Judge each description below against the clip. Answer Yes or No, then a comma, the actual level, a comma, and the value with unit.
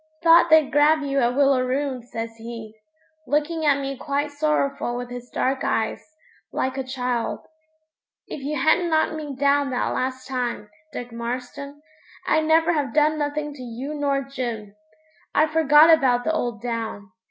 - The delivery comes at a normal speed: Yes, average, 160 wpm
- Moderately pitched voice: No, very high, 275 Hz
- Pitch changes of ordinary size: Yes, average, 3.4 semitones